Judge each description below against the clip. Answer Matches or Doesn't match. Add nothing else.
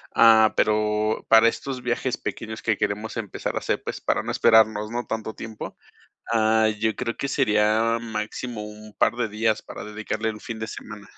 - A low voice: Matches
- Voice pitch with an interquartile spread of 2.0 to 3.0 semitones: Doesn't match